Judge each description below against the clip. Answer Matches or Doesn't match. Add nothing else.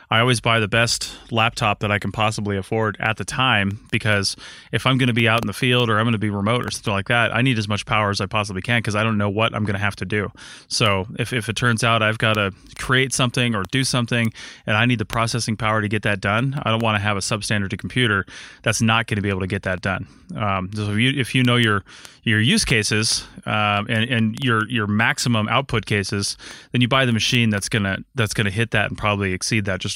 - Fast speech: Matches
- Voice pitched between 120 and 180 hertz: Doesn't match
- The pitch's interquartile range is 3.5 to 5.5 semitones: Doesn't match